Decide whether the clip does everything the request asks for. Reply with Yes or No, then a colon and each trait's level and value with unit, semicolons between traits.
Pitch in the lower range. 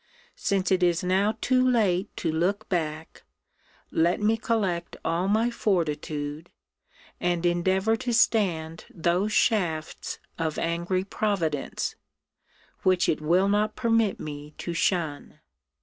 No: medium, 180 Hz